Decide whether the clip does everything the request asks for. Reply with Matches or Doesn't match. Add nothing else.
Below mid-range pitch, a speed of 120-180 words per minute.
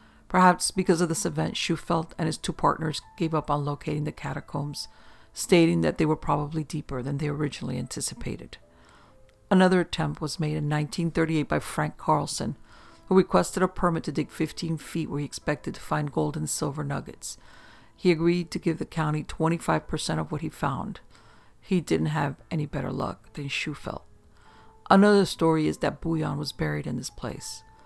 Doesn't match